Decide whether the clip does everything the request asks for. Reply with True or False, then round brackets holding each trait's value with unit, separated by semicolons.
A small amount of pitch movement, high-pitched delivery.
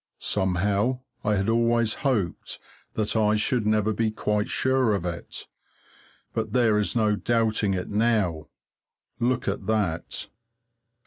False (2.3 semitones; 110 Hz)